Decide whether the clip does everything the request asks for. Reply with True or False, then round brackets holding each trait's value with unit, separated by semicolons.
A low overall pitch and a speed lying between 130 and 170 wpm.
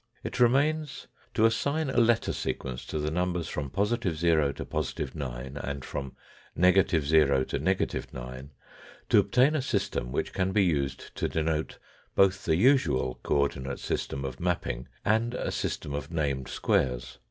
True (80 Hz; 155 wpm)